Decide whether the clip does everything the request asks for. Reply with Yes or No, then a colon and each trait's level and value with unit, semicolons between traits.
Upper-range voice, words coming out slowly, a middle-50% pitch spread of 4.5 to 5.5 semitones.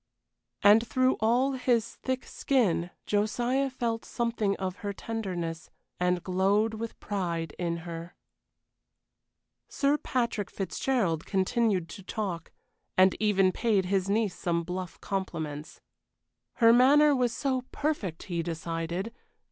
Yes: high, 205 Hz; slow, 120 wpm; average, 4.9 semitones